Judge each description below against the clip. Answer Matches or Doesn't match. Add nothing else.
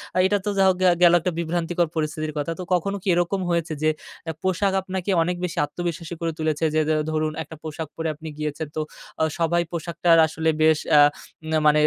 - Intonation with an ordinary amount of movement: Doesn't match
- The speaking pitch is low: Doesn't match